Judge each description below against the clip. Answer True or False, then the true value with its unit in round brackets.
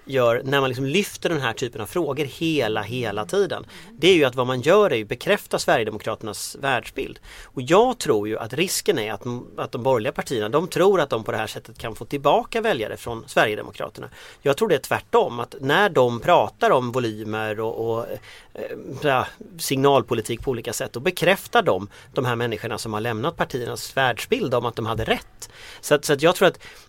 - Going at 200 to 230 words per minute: True (205 wpm)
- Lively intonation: True (6.3 semitones)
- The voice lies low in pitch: True (130 Hz)